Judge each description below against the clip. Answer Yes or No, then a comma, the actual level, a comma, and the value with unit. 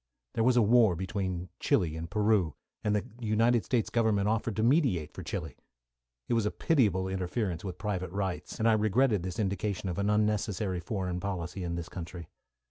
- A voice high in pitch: No, low, 100 Hz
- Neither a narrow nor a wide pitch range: Yes, average, 3.4 semitones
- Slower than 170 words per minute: No, average, 185 wpm